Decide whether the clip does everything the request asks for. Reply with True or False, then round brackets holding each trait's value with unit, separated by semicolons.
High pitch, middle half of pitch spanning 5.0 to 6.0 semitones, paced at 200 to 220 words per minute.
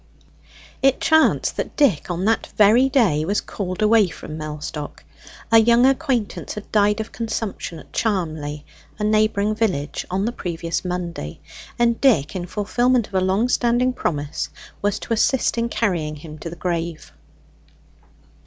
False (205 Hz; 5.6 semitones; 155 wpm)